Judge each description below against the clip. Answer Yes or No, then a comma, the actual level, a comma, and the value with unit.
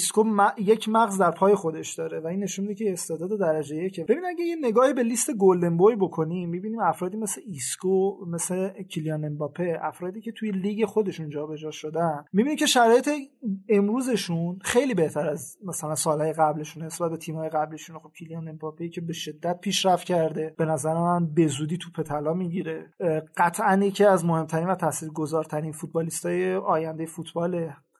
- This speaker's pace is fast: Yes, fast, 165 wpm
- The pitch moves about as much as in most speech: Yes, average, 3.9 semitones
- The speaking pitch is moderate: Yes, medium, 170 Hz